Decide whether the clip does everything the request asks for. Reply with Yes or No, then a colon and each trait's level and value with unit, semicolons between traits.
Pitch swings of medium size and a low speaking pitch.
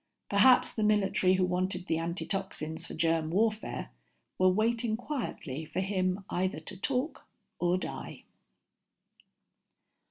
No: average, 3.4 semitones; medium, 185 Hz